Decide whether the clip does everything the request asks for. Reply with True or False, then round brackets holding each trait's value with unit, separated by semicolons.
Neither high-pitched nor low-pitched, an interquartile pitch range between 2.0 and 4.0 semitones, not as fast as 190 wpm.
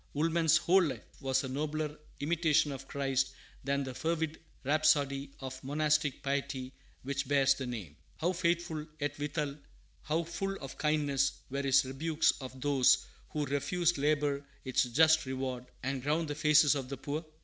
True (145 Hz; 2.5 semitones; 160 wpm)